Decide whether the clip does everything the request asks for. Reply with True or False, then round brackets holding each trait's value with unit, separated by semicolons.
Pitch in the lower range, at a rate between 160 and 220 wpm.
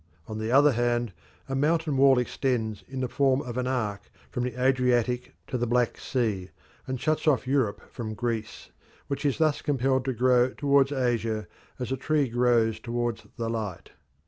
True (125 Hz; 175 wpm)